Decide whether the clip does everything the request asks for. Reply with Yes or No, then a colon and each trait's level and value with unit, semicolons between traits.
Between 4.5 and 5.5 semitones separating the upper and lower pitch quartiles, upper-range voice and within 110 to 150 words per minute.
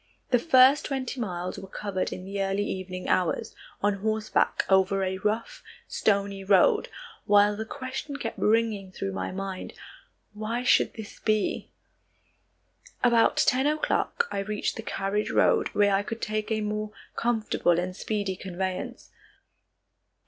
No: average, 2.8 semitones; high, 205 Hz; average, 140 wpm